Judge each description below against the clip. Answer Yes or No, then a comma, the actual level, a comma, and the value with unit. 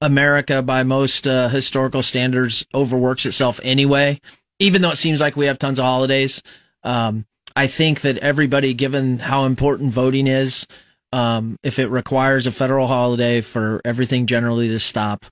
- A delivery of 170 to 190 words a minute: No, average, 160 wpm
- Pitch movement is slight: Yes, narrow, 1.9 semitones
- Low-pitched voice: Yes, low, 130 Hz